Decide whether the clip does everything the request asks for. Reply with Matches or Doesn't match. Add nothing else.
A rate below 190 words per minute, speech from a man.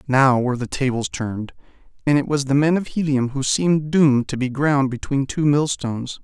Doesn't match